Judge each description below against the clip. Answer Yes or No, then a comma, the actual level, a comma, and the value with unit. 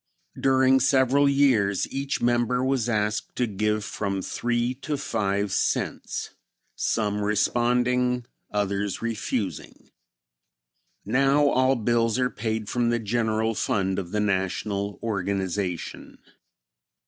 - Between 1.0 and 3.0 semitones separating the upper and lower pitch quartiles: No, average, 3.6 semitones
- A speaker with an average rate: No, slow, 110 wpm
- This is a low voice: Yes, low, 115 Hz